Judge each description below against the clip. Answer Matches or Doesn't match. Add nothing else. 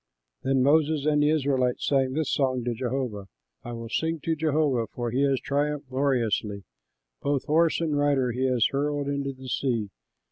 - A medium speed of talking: Matches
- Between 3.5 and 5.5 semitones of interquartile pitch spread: Doesn't match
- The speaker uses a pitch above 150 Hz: Doesn't match